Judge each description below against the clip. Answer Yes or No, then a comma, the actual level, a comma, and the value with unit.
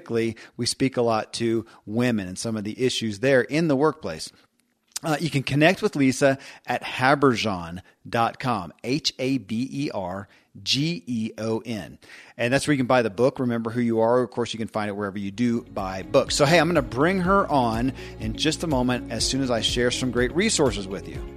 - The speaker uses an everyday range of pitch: Yes, average, 3.7 semitones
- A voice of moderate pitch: No, low, 120 Hz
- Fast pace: Yes, fast, 215 wpm